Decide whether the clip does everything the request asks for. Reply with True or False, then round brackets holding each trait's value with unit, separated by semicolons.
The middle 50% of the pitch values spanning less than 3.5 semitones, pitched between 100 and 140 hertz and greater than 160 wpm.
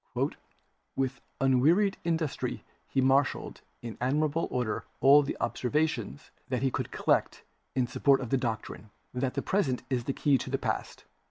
False (2.8 semitones; 135 Hz; 155 wpm)